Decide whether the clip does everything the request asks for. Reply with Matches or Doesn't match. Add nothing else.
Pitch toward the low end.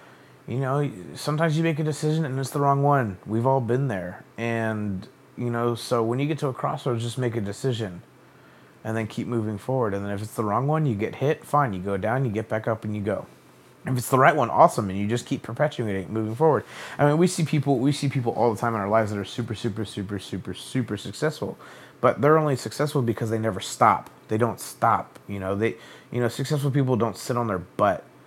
Matches